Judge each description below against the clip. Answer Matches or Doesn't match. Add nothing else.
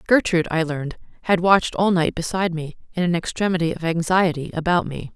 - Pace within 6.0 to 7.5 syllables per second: Matches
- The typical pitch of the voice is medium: Matches